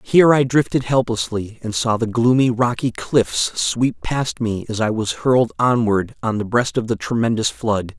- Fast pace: No, average, 190 wpm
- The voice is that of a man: Yes, male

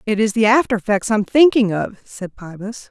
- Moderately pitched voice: No, high, 215 Hz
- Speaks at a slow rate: No, fast, 205 wpm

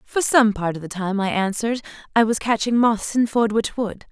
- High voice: Yes, high, 220 Hz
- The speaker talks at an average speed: No, fast, 220 wpm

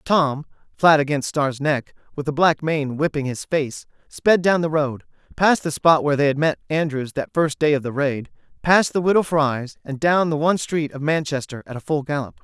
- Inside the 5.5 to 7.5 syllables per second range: No, 5.1 syllables/s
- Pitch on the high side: No, medium, 150 Hz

